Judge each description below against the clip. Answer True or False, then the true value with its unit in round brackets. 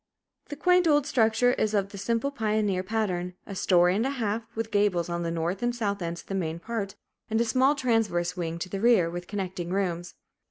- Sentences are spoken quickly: True (215 wpm)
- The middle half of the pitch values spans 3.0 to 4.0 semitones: False (4.5 semitones)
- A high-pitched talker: True (205 Hz)